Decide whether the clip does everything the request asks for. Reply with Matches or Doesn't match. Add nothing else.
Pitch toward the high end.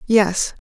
Matches